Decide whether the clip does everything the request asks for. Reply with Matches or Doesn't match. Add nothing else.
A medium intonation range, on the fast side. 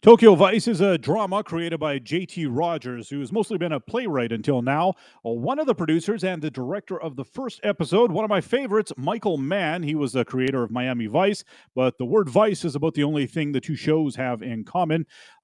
Doesn't match